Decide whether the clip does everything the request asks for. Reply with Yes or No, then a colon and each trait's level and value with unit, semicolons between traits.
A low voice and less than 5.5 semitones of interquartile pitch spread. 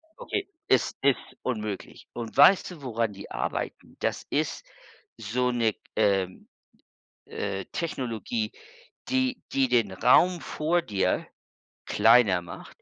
No: low, 120 Hz; wide, 6.8 semitones